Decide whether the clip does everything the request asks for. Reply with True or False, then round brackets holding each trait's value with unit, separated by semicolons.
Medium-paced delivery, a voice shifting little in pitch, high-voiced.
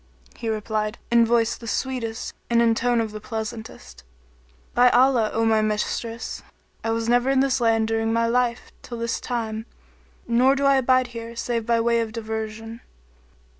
True (170 wpm; 1.4 semitones; 230 Hz)